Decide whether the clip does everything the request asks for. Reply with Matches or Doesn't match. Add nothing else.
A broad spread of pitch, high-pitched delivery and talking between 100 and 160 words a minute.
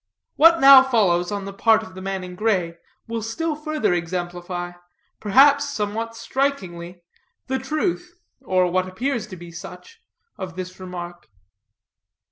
Matches